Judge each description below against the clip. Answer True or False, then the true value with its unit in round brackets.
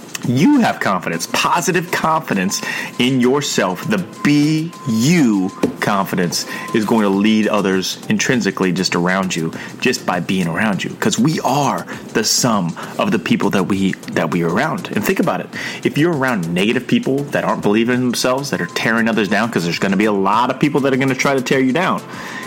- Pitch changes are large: True (6.0 semitones)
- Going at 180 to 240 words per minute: True (205 wpm)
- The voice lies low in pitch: True (120 Hz)